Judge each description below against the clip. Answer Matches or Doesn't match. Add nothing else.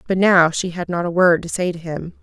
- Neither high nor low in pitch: Matches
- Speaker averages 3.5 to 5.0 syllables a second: Doesn't match